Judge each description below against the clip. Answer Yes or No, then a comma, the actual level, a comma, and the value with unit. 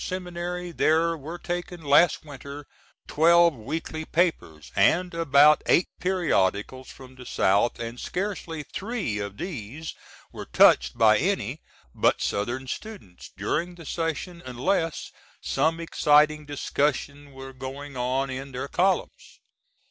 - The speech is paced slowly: Yes, slow, 125 wpm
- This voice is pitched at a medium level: Yes, medium, 150 Hz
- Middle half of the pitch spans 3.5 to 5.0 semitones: Yes, average, 4.6 semitones